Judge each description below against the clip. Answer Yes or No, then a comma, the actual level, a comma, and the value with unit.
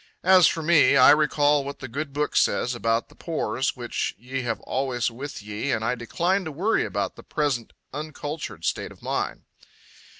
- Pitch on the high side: No, medium, 140 Hz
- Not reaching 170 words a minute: No, average, 185 wpm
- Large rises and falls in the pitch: No, average, 4.3 semitones